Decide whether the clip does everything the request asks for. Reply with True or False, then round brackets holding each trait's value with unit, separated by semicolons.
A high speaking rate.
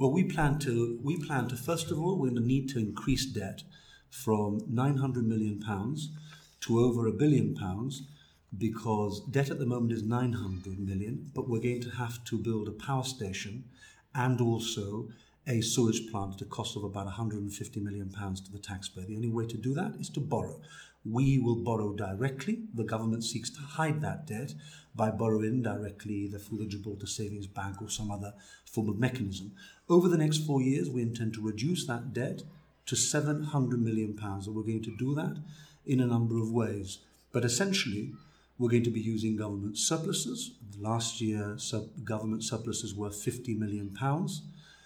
False (185 wpm)